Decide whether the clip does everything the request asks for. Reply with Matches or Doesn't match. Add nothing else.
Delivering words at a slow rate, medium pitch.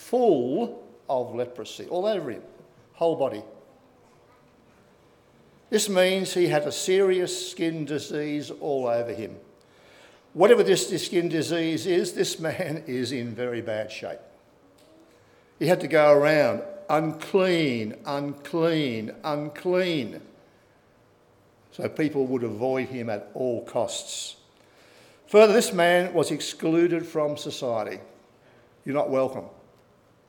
Matches